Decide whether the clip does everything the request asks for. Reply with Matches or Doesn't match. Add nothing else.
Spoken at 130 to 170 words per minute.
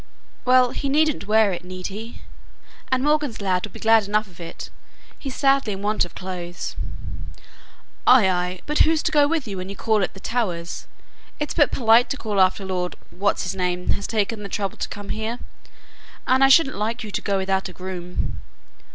Doesn't match